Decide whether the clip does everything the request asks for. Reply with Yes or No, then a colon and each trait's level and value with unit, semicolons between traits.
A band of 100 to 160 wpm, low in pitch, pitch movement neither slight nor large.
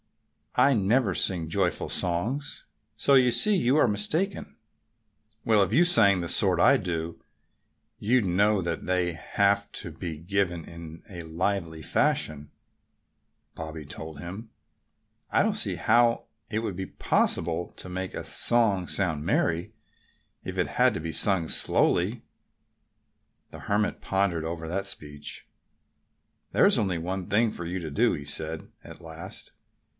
Yes: average, 145 wpm; very low, 90 Hz; average, 4.1 semitones